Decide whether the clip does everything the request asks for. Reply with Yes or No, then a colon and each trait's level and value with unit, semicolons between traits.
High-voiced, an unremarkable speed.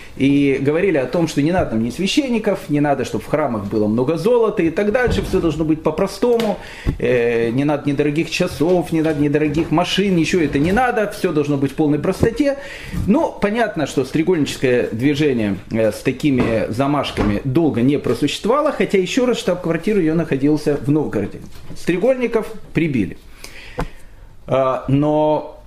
No: medium, 150 Hz; average, 150 wpm